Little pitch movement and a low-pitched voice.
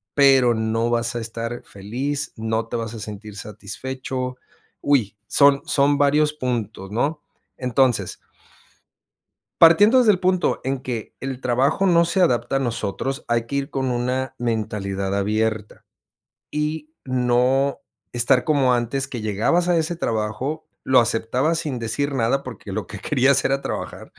No: average, 3.7 semitones; low, 125 Hz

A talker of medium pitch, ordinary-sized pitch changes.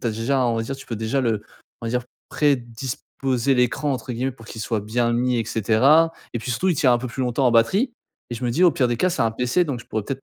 No: low, 125 Hz; average, 3.0 semitones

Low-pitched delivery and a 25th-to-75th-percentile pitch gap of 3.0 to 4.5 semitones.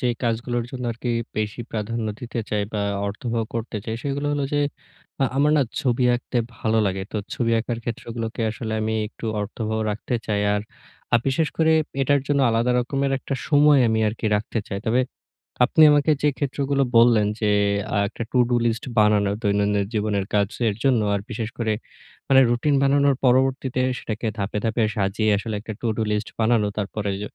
Yes: low, 115 Hz; average, 3.5 semitones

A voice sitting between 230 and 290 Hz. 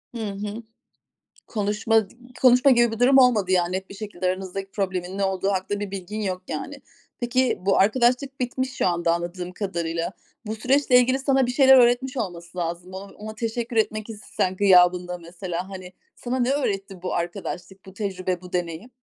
No: high, 200 Hz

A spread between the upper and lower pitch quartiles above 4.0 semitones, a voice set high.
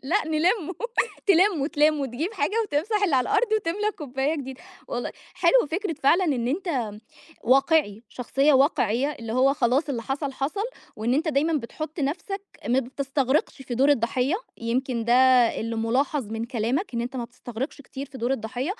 Yes: average, 4.6 semitones; very high, 275 Hz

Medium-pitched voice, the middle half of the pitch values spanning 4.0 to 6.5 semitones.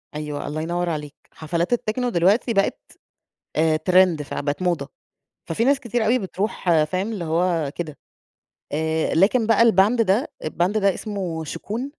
Yes: medium, 180 Hz; wide, 5.4 semitones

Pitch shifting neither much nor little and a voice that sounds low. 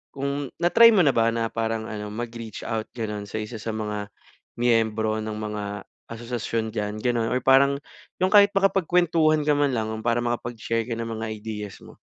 Yes: average, 3.8 semitones; low, 115 Hz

